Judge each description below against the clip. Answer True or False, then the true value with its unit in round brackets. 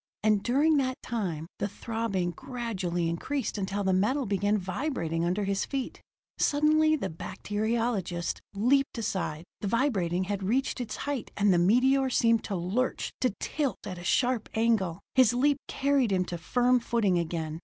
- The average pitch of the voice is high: True (215 Hz)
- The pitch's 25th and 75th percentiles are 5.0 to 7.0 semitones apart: True (5.6 semitones)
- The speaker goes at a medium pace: True (160 wpm)